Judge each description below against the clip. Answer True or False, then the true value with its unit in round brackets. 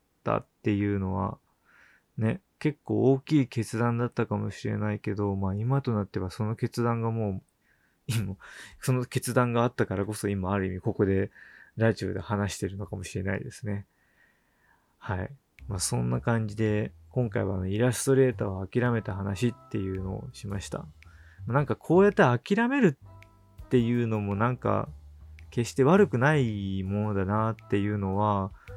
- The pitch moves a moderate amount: True (3.6 semitones)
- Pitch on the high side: False (105 Hz)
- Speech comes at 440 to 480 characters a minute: False (320 characters per minute)